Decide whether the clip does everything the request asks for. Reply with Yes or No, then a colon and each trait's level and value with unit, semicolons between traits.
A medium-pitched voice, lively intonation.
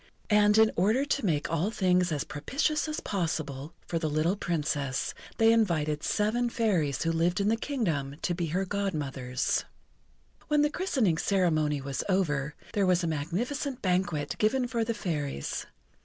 Yes: medium, 180 Hz; wide, 6.5 semitones